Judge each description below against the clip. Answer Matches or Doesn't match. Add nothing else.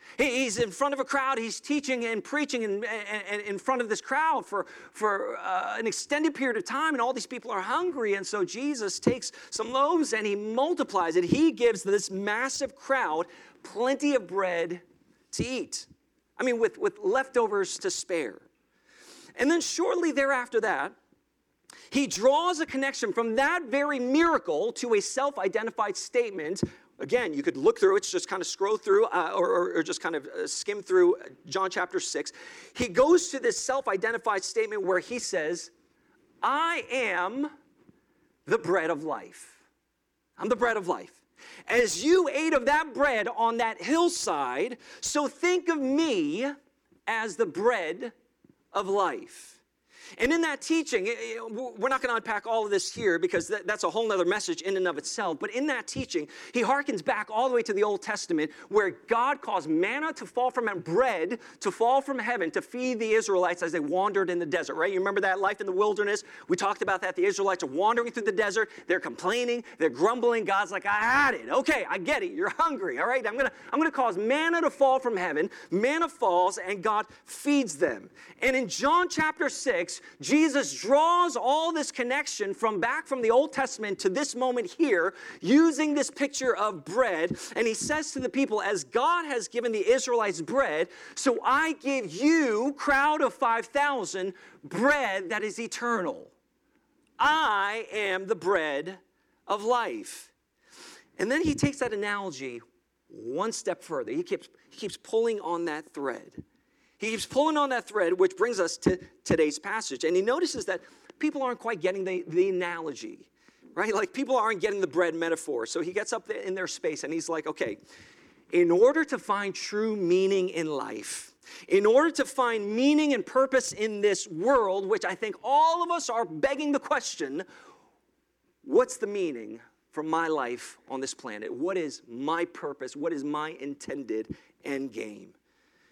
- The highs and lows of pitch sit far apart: Matches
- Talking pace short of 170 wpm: Doesn't match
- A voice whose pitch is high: Matches